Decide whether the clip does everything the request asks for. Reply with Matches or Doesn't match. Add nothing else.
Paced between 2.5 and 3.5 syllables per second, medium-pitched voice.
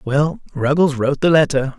Doesn't match